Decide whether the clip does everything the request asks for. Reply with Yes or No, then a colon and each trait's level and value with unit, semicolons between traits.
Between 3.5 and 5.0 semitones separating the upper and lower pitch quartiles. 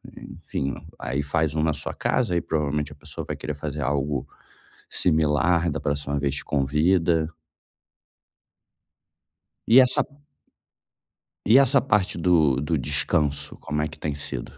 No: average, 2.9 semitones